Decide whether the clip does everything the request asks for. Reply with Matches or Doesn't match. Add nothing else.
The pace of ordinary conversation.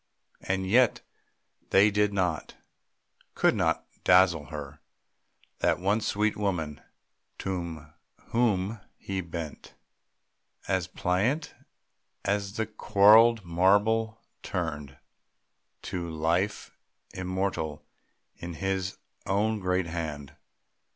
Doesn't match